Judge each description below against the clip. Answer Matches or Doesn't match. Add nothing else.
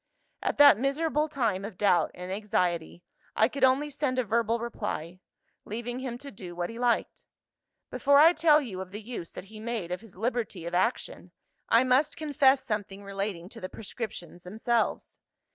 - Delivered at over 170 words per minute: Matches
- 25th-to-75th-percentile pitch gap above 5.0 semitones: Matches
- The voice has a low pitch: Doesn't match